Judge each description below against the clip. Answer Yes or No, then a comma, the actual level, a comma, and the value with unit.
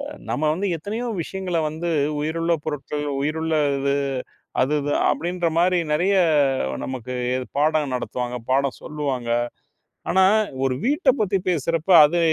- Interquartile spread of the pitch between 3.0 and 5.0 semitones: Yes, average, 4.2 semitones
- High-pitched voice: No, medium, 155 Hz